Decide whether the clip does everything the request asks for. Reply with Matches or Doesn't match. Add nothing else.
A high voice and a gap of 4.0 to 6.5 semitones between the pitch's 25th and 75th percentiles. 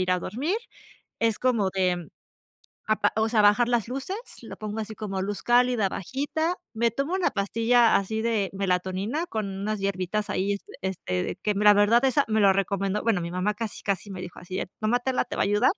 Doesn't match